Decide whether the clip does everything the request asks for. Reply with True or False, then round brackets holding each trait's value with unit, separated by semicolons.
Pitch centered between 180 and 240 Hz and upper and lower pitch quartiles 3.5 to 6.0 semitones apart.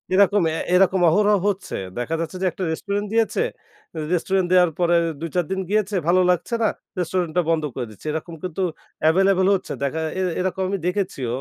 False (185 Hz; 2.7 semitones)